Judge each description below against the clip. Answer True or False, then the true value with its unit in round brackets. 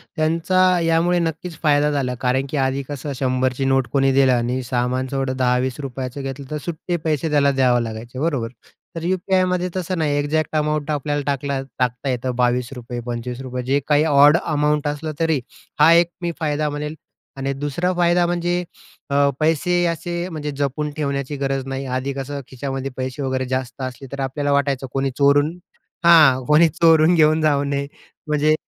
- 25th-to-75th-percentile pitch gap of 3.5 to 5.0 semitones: False (3.1 semitones)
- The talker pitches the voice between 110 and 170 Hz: True (140 Hz)